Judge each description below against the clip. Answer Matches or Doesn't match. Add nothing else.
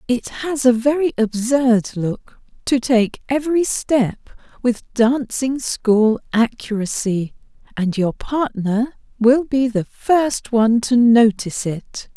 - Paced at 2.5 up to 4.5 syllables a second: Matches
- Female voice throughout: Matches